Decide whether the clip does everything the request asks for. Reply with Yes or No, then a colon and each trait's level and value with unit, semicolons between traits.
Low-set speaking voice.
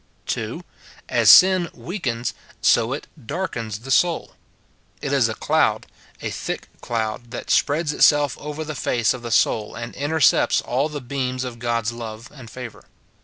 Yes: low, 125 Hz